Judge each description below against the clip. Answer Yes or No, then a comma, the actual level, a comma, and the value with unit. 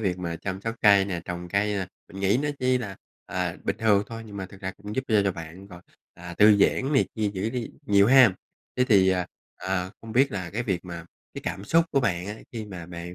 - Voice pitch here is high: No, low, 100 Hz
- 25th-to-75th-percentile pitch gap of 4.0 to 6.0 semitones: No, average, 3.4 semitones